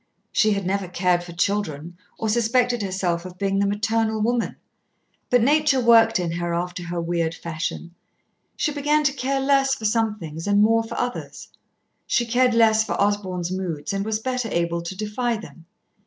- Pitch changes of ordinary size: Yes, average, 4.9 semitones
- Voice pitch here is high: Yes, high, 210 Hz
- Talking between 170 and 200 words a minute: Yes, average, 180 wpm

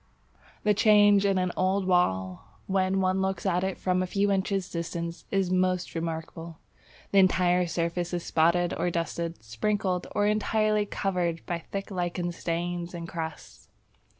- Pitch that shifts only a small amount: Yes, narrow, 2.3 semitones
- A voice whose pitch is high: No, medium, 180 Hz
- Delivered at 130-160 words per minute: Yes, average, 150 wpm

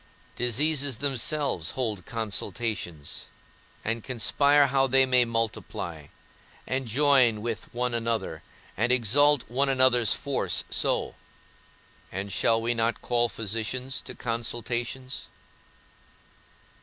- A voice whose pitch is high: No, low, 120 Hz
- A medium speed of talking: No, slow, 105 wpm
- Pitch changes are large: No, average, 2.8 semitones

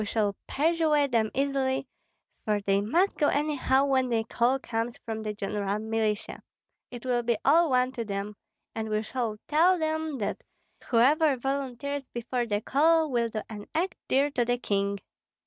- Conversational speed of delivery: Yes, average, 170 wpm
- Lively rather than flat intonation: No, average, 4.5 semitones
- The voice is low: No, high, 245 Hz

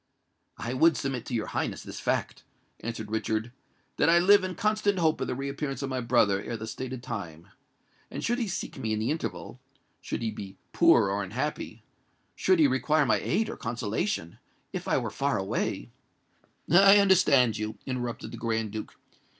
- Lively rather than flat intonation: Yes, wide, 6.2 semitones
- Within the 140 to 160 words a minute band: No, average, 170 wpm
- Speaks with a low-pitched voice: Yes, low, 125 Hz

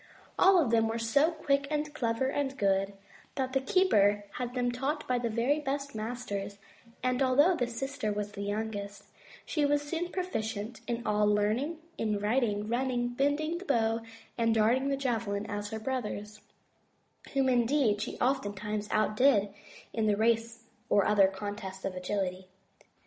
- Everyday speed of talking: Yes, average, 160 wpm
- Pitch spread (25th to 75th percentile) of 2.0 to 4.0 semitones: No, average, 4.6 semitones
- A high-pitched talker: Yes, high, 230 Hz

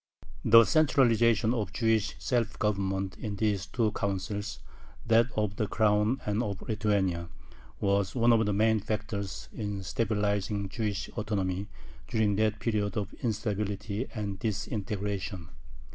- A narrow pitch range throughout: Yes, narrow, 1.8 semitones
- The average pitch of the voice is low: Yes, low, 105 Hz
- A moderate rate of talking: No, slow, 130 wpm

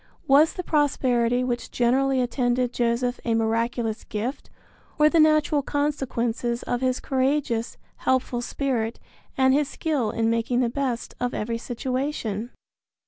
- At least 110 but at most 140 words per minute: Yes, slow, 135 wpm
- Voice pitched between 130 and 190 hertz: No, very high, 250 Hz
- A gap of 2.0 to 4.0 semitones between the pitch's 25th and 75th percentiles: Yes, narrow, 2.6 semitones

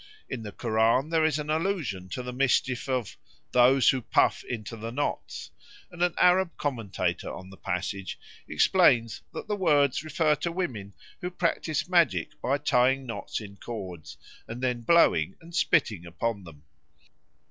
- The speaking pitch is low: Yes, low, 125 Hz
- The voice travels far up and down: Yes, wide, 6.5 semitones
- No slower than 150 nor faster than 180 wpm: Yes, average, 160 wpm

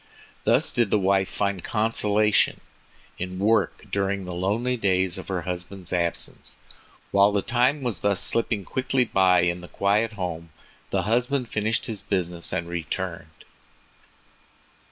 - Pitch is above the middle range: No, low, 100 Hz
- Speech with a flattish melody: No, average, 3.3 semitones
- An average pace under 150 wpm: Yes, average, 140 wpm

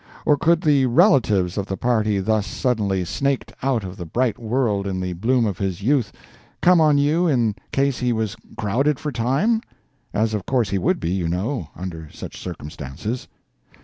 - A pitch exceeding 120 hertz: No, low, 115 Hz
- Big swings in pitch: Yes, wide, 6.0 semitones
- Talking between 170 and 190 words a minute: Yes, average, 180 wpm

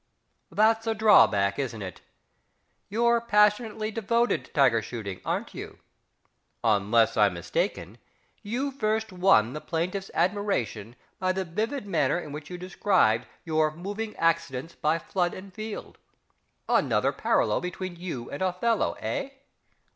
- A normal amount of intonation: No, wide, 8.7 semitones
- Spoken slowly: Yes, slow, 130 wpm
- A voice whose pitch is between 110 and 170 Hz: No, medium, 180 Hz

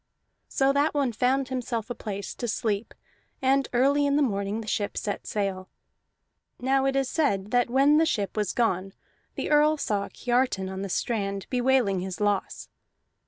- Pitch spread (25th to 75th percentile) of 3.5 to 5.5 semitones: Yes, average, 5.1 semitones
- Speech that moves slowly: No, average, 170 wpm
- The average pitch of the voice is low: No, high, 240 Hz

